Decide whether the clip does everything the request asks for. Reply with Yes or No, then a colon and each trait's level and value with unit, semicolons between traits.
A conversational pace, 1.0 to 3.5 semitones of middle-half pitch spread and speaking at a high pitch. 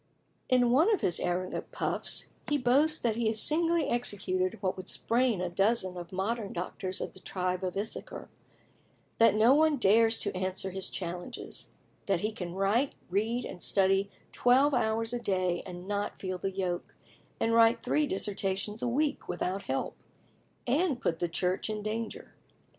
No: average, 170 wpm; average, 4.5 semitones; high, 205 Hz